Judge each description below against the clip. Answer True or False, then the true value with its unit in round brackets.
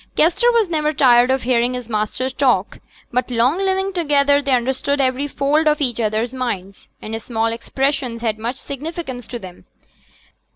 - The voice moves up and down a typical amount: True (3.6 semitones)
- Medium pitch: False (255 Hz)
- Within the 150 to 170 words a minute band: True (165 wpm)